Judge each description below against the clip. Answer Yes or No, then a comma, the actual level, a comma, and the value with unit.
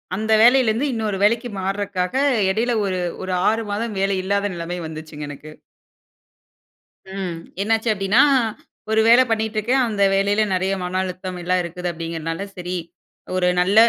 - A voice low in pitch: No, high, 195 Hz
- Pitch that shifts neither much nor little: Yes, average, 3.5 semitones